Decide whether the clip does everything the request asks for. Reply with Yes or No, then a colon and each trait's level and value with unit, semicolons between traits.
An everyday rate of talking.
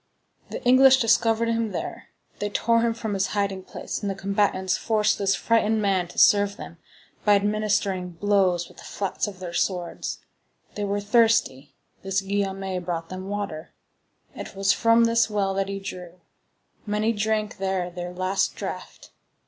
Yes: average, 165 wpm